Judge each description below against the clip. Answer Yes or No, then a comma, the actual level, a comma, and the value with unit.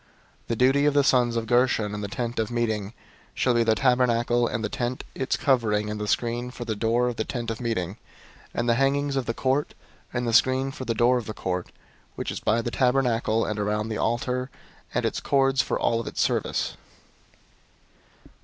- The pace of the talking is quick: Yes, fast, 215 wpm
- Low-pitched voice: Yes, low, 120 Hz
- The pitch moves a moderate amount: No, narrow, 2.2 semitones